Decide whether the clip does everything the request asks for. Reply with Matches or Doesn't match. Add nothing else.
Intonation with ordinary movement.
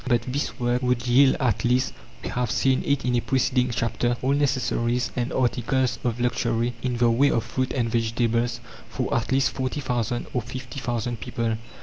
Doesn't match